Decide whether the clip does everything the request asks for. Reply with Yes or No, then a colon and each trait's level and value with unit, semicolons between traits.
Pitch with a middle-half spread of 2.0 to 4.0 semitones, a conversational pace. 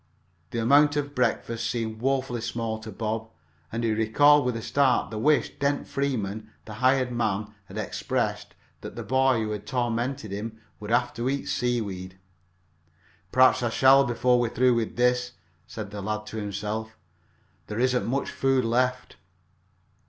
Yes: average, 2.8 semitones; average, 160 wpm